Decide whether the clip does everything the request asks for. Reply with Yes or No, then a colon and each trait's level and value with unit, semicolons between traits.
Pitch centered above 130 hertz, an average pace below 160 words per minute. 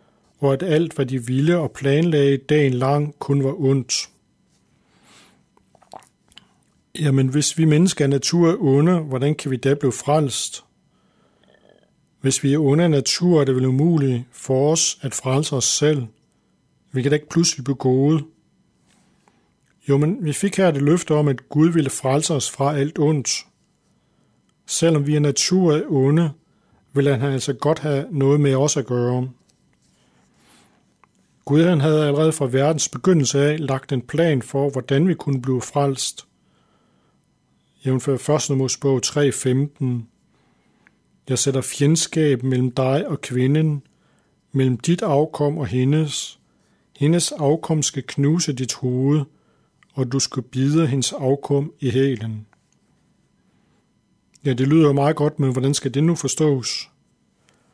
Yes: medium, 140 Hz; slow, 145 wpm